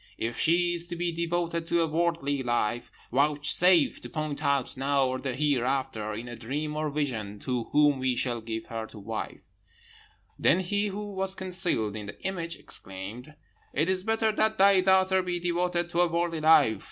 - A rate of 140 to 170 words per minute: No, average, 180 wpm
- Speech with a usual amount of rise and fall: No, wide, 6.0 semitones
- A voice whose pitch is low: No, medium, 155 Hz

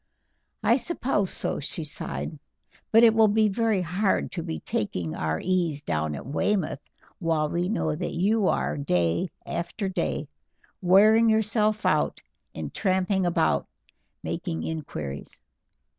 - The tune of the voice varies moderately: No, wide, 5.7 semitones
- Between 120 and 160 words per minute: Yes, slow, 135 wpm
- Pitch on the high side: No, medium, 180 Hz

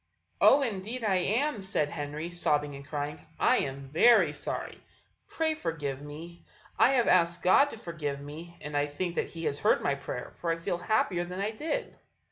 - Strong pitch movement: Yes, wide, 5.7 semitones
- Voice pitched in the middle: Yes, medium, 170 Hz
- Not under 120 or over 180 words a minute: No, average, 190 wpm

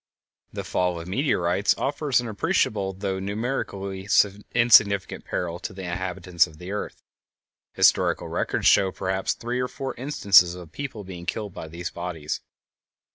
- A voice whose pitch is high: No, very low, 95 Hz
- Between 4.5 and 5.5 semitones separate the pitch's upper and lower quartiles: No, average, 3.5 semitones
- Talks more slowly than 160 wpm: Yes, average, 145 wpm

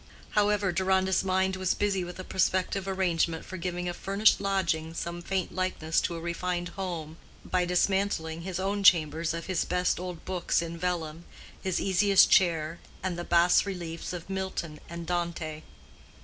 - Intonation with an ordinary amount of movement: No, narrow, 2.0 semitones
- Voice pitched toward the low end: No, medium, 180 Hz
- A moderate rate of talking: Yes, average, 165 wpm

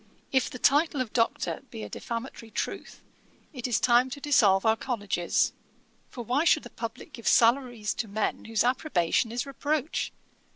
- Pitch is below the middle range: No, high, 240 Hz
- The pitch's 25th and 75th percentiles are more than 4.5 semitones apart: No, average, 3.1 semitones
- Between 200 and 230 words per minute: No, average, 165 wpm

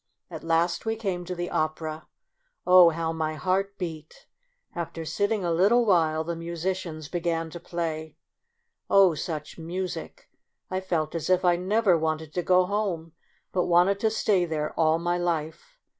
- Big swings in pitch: No, narrow, 2.6 semitones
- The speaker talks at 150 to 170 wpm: Yes, average, 160 wpm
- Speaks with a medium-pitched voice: Yes, medium, 170 Hz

